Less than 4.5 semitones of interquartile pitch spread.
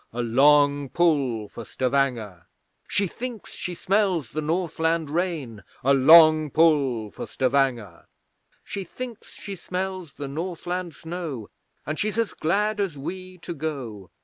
No: average, 5.3 semitones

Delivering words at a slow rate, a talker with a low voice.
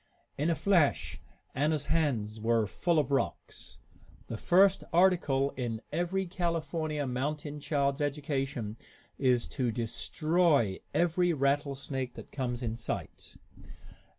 No: slow, 115 wpm; medium, 145 Hz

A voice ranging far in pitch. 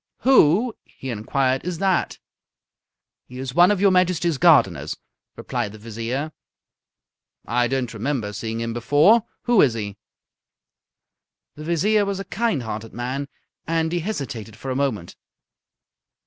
Yes: wide, 7.4 semitones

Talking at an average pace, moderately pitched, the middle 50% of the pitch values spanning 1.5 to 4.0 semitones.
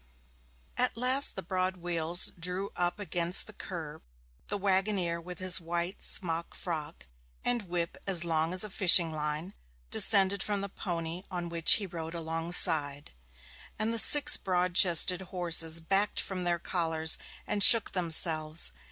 Yes: average, 150 wpm; medium, 175 Hz; narrow, 2.6 semitones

